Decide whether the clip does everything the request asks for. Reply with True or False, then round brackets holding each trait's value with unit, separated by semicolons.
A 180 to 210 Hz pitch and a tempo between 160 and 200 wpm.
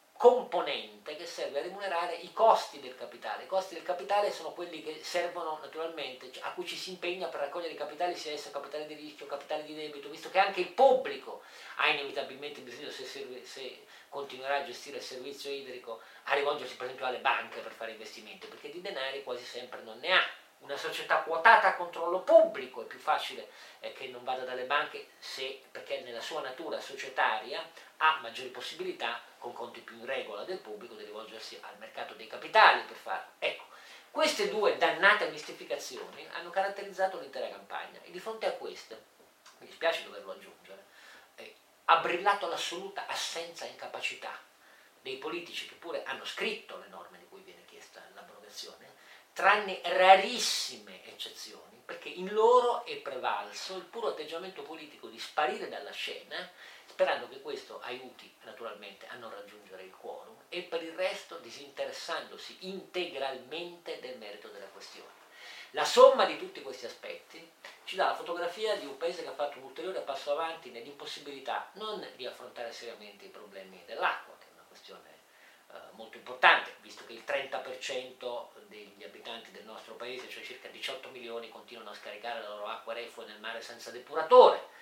True (185 Hz; 170 wpm)